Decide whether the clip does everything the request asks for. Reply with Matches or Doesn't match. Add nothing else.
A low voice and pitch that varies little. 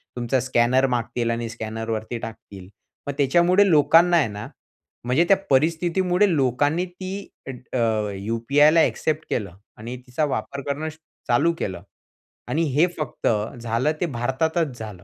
Doesn't match